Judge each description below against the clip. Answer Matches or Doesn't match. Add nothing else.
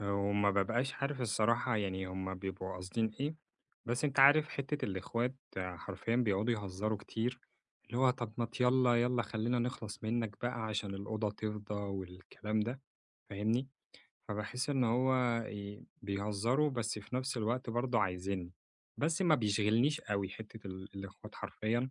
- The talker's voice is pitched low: Matches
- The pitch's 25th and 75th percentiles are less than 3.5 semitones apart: Doesn't match